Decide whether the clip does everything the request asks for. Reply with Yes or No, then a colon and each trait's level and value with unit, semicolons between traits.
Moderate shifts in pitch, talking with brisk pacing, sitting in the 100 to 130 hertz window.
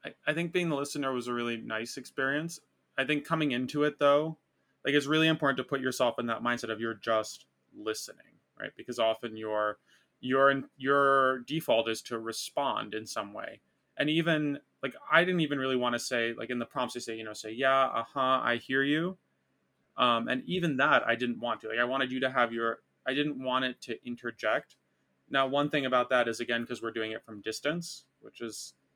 Yes: average, 3.7 semitones; fast, 220 wpm; low, 125 Hz